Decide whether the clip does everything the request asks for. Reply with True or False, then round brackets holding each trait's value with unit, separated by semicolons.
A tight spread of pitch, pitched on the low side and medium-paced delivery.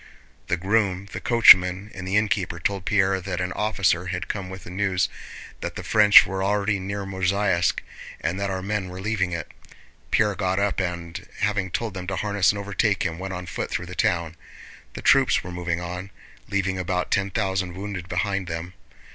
True (2.0 semitones; 95 Hz; 190 wpm)